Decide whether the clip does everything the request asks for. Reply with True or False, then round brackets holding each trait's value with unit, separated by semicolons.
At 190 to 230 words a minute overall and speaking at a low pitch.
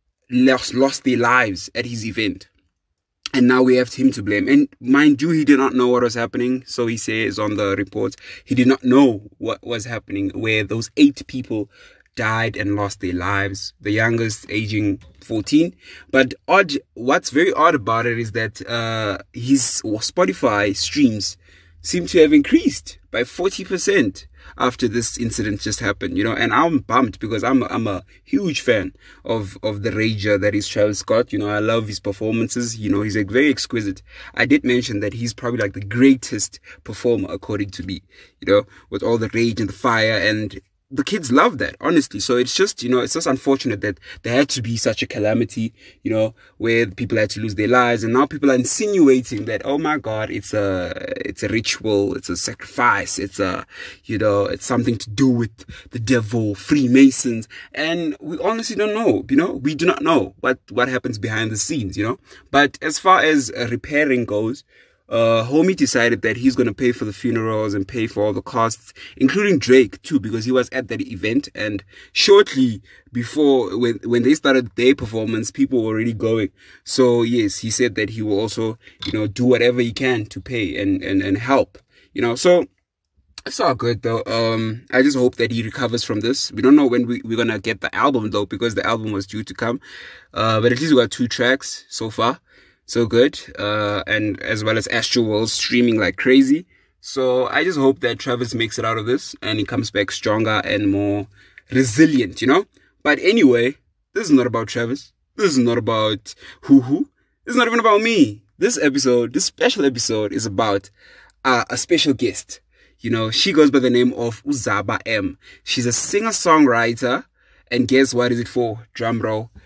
True (200 wpm; 115 Hz)